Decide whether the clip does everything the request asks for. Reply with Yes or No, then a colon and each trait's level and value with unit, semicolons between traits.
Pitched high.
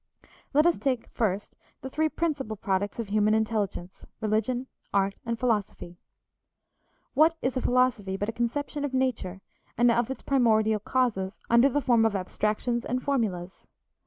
Yes: high, 230 Hz